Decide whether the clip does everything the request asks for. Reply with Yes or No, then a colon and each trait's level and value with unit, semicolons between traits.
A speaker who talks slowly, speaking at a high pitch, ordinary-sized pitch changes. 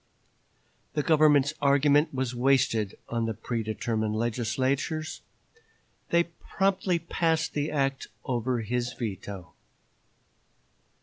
No: slow, 90 wpm; low, 130 Hz; average, 4.8 semitones